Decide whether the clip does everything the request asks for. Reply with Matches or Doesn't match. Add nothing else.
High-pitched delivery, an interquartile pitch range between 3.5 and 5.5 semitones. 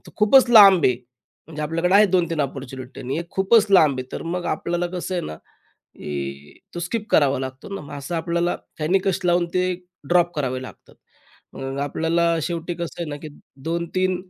Doesn't match